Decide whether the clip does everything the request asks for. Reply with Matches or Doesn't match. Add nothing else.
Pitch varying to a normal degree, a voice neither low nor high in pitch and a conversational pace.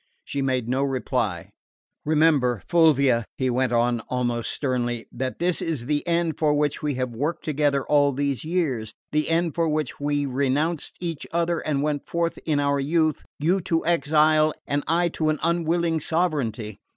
Matches